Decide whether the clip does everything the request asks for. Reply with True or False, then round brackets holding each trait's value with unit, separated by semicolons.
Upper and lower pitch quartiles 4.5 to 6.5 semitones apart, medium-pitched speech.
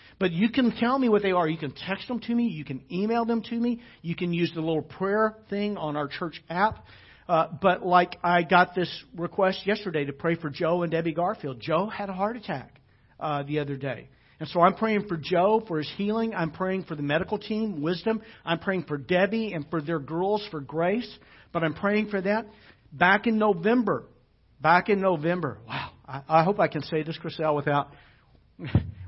True (5.2 semitones; 175 Hz)